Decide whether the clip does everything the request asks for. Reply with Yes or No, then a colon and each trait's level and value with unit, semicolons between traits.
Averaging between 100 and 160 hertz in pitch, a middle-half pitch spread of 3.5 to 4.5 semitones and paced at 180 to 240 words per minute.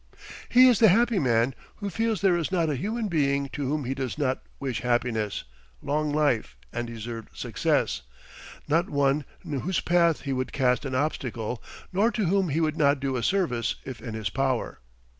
No: medium, 140 Hz; wide, 5.6 semitones; average, 190 wpm